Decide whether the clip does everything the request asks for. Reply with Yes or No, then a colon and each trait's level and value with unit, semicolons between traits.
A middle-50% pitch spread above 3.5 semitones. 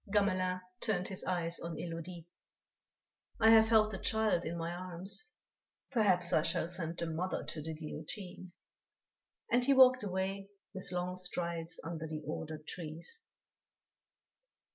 No: average, 3.0 semitones